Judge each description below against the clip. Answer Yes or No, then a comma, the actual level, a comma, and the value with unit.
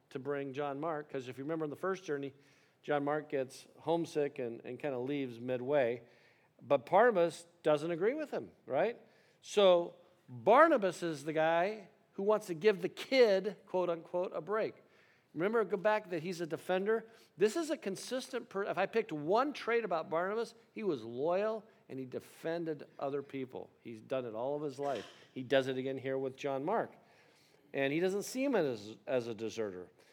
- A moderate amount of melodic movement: No, wide, 6.3 semitones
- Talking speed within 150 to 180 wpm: No, average, 190 wpm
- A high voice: No, medium, 165 Hz